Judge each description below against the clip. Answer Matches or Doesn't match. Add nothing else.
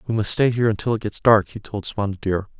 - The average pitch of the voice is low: Matches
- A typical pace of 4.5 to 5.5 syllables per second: Doesn't match